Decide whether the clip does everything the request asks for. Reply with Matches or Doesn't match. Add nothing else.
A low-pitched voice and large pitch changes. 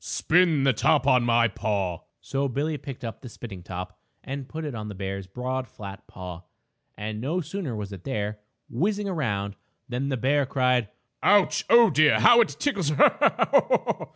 Matches